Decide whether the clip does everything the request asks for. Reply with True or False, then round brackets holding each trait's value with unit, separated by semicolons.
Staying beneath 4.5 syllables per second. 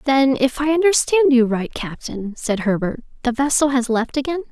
False (5.0 syllables/s)